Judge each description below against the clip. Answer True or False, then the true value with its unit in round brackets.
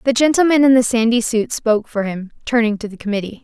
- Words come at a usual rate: False (225 wpm)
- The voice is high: True (230 Hz)